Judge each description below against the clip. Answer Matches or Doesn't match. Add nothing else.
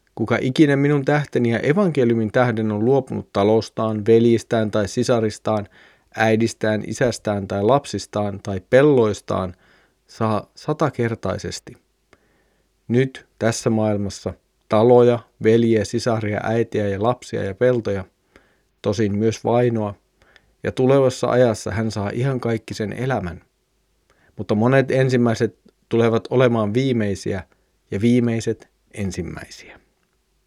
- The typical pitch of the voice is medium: Doesn't match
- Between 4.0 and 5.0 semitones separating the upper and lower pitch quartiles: Doesn't match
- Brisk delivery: Doesn't match